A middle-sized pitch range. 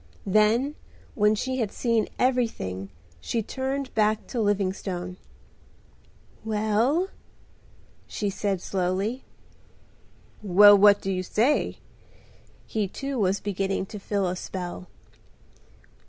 Yes: average, 3.4 semitones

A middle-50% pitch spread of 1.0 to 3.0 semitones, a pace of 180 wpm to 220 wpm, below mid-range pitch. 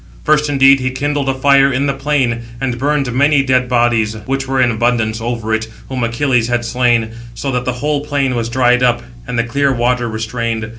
Yes: narrow, 2.6 semitones; fast, 205 wpm; low, 125 Hz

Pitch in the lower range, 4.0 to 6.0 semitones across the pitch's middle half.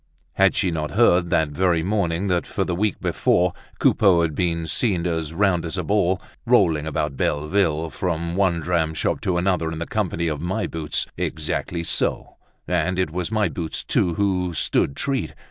No: very low, 85 Hz; narrow, 2.6 semitones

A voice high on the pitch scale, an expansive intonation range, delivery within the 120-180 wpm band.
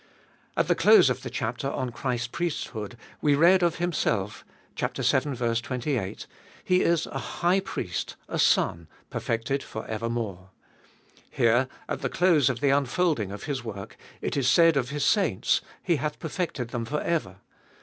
No: low, 130 Hz; wide, 5.9 semitones; average, 160 wpm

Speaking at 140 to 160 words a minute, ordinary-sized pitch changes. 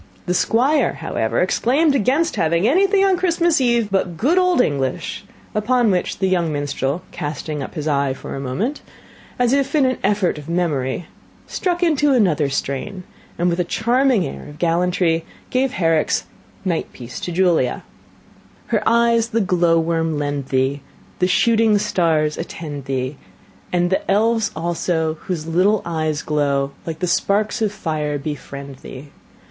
No: average, 155 wpm; wide, 7.4 semitones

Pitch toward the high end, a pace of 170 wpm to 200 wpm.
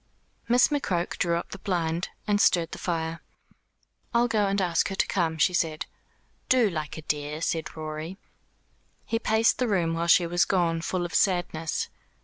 No: medium, 175 Hz; average, 175 wpm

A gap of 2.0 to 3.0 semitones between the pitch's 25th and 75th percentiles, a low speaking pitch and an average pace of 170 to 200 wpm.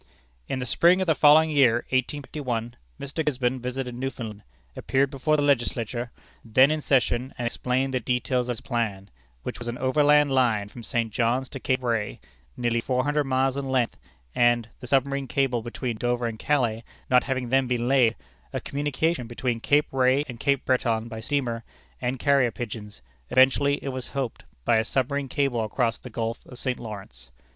Yes: narrow, 2.5 semitones; low, 125 Hz; average, 180 wpm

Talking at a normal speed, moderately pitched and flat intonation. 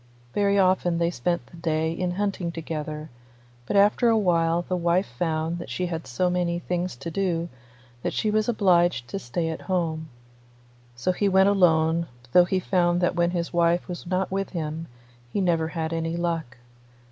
Yes: average, 180 wpm; medium, 175 Hz; narrow, 2.0 semitones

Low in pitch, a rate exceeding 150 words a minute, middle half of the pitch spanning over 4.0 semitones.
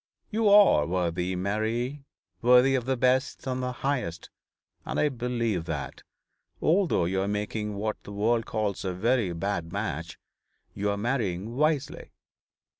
No: low, 110 Hz; average, 145 wpm; average, 5.1 semitones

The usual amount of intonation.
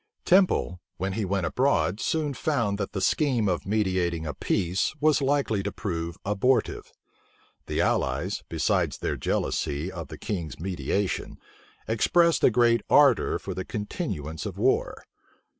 No: wide, 6.4 semitones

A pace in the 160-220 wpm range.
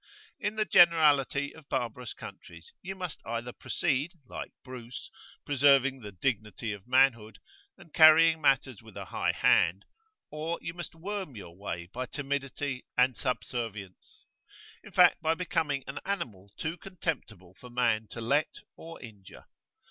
No: average, 145 wpm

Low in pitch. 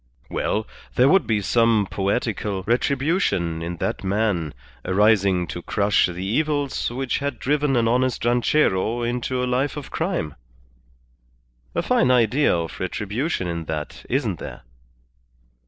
Yes: low, 115 Hz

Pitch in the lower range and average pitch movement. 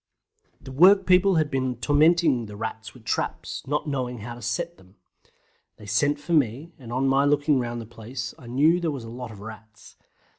Yes: low, 130 Hz; average, 4.7 semitones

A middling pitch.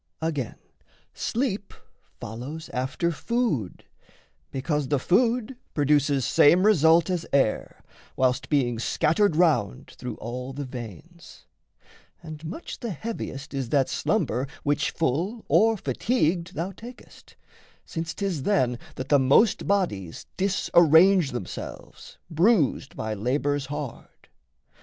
Yes: medium, 150 Hz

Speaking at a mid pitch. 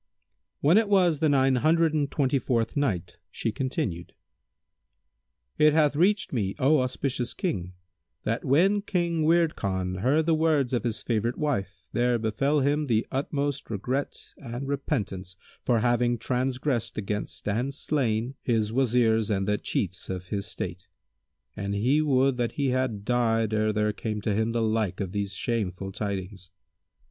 No: low, 120 Hz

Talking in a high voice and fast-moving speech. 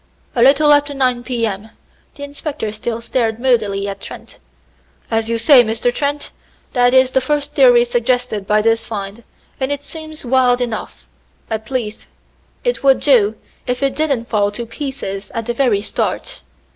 No: high, 245 Hz; average, 170 wpm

